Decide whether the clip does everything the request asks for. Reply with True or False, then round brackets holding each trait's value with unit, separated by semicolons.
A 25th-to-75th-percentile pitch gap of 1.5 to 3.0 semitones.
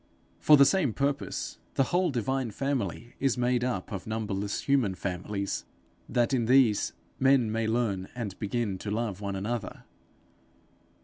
False (4.6 semitones)